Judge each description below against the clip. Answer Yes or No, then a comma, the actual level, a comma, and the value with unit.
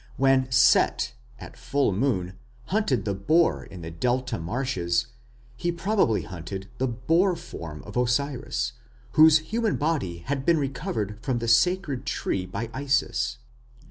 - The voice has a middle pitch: No, low, 125 Hz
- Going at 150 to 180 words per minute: No, average, 140 wpm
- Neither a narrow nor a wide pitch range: No, wide, 6.6 semitones